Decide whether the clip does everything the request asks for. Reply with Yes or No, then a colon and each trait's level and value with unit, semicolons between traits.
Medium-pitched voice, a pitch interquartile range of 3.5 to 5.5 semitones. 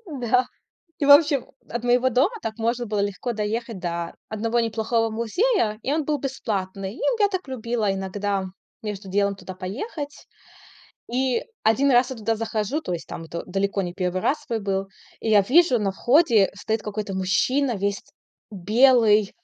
No: high, 220 Hz; average, 4.2 semitones